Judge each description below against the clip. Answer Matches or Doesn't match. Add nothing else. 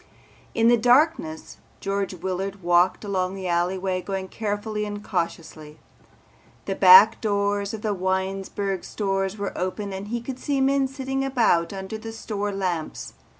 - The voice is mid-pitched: Doesn't match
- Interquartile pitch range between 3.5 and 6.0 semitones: Doesn't match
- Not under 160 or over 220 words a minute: Doesn't match